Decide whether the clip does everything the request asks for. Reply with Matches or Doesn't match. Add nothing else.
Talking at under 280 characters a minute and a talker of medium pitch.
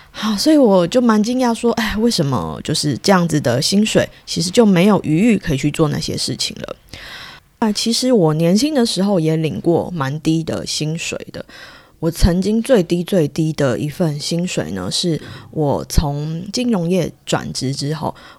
Matches